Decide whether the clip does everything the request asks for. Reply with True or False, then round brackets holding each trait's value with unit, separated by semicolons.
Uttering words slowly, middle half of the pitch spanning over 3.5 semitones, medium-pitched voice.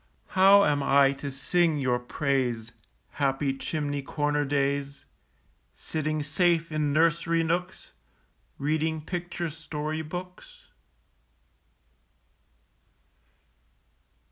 False (85 wpm; 3.0 semitones; 150 Hz)